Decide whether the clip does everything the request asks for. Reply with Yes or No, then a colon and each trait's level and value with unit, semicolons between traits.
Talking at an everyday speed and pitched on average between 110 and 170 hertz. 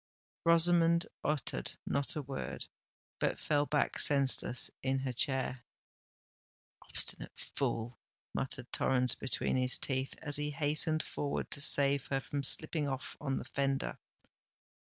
No: slow, 130 wpm; medium, 140 Hz